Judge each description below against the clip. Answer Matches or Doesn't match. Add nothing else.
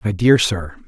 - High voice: Doesn't match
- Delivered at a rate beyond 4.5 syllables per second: Doesn't match